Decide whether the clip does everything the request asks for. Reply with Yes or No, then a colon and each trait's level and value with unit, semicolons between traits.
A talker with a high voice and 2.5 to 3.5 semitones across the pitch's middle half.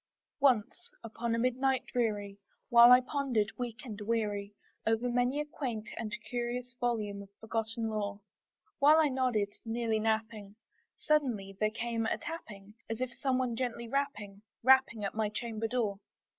Yes: high, 230 Hz; average, 2.9 semitones